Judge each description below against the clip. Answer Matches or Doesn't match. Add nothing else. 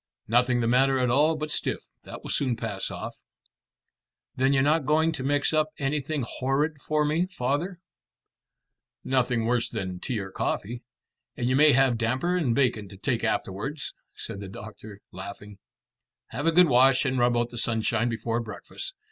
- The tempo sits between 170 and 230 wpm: Matches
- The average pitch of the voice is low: Matches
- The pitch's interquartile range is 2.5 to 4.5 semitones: Matches